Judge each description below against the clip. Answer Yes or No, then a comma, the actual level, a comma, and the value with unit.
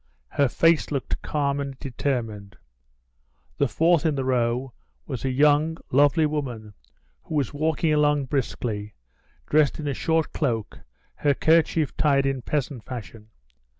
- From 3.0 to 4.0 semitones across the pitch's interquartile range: Yes, average, 3.4 semitones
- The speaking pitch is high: No, medium, 140 Hz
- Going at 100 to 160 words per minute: Yes, average, 140 wpm